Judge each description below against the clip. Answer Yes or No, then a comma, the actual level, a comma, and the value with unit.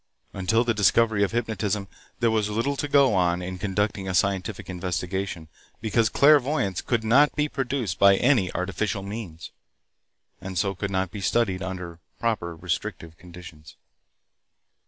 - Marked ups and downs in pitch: No, average, 4.0 semitones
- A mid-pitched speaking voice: No, low, 100 Hz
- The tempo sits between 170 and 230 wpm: No, average, 145 wpm